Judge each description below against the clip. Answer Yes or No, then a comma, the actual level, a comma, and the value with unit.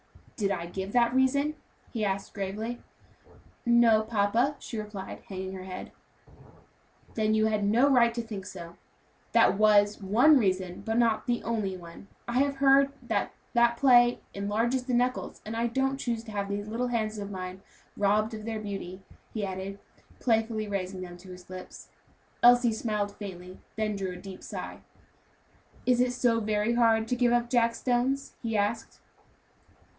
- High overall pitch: Yes, high, 220 Hz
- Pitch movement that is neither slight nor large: Yes, average, 3.3 semitones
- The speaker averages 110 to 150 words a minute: No, average, 170 wpm